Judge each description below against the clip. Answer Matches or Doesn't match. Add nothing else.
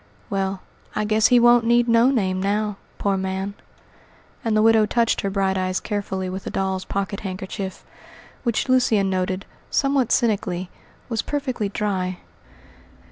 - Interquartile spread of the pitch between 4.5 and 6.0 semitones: Doesn't match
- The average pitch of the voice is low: Doesn't match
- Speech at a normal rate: Matches